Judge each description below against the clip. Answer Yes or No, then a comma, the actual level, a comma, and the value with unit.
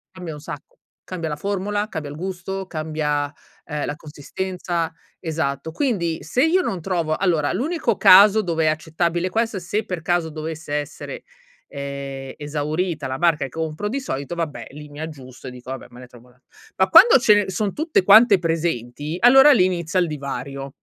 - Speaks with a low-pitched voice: No, medium, 165 Hz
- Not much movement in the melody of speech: No, average, 4.5 semitones